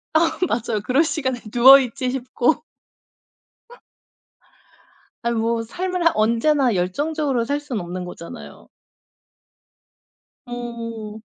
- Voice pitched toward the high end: Yes, high, 245 Hz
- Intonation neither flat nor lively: Yes, average, 4.2 semitones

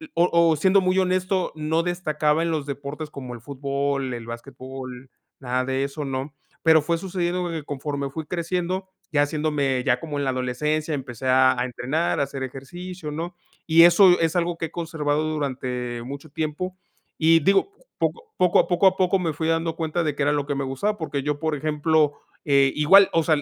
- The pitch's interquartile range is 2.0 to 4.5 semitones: Yes, average, 3.6 semitones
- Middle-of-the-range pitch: Yes, medium, 150 Hz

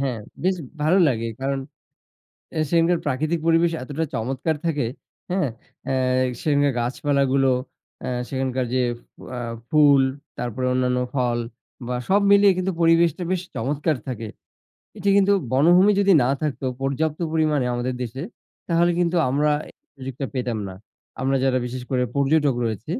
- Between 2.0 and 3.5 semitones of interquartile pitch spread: No, average, 4.3 semitones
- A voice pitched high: No, medium, 140 Hz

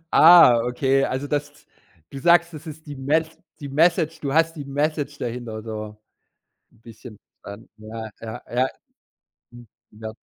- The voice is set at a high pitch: No, low, 135 Hz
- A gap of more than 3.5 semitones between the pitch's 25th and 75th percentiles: Yes, average, 5.1 semitones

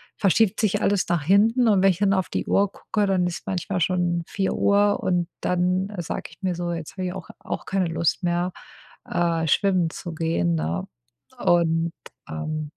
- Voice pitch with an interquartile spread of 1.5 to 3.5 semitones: Yes, average, 2.7 semitones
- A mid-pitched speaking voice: Yes, medium, 180 Hz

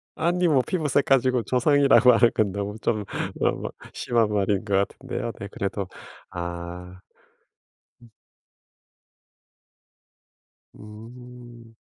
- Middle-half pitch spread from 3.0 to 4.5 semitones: Yes, average, 4.1 semitones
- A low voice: Yes, low, 115 Hz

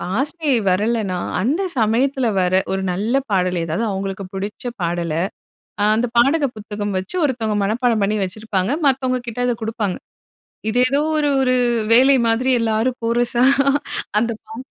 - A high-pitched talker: Yes, high, 225 Hz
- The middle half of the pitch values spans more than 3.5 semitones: Yes, average, 4.2 semitones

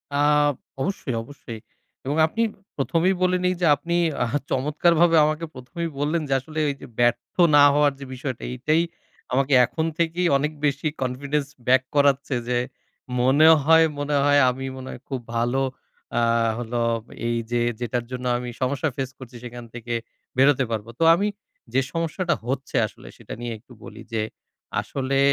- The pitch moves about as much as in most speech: Yes, average, 3.9 semitones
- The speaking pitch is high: No, low, 135 Hz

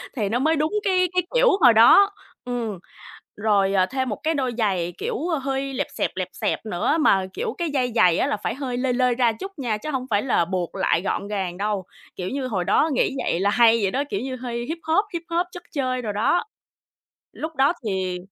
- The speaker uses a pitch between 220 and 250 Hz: Yes, high, 245 Hz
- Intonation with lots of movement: Yes, wide, 6.0 semitones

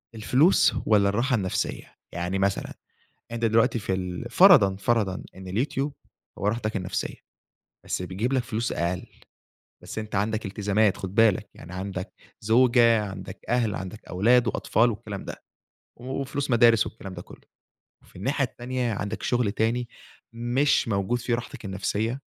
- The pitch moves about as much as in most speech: Yes, average, 3.7 semitones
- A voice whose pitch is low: Yes, low, 110 Hz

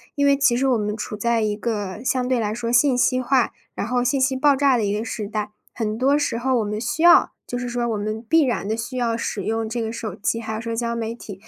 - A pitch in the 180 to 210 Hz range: No, high, 235 Hz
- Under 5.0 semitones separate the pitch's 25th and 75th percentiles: Yes, average, 2.7 semitones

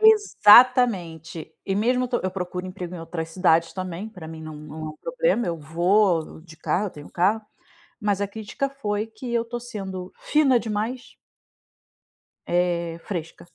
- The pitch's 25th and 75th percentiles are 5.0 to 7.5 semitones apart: Yes, wide, 5.5 semitones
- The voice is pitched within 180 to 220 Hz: Yes, high, 190 Hz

